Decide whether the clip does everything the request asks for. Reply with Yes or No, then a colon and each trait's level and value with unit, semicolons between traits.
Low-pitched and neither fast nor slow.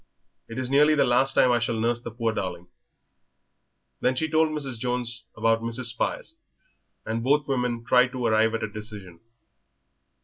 Yes: low, 120 Hz; average, 170 wpm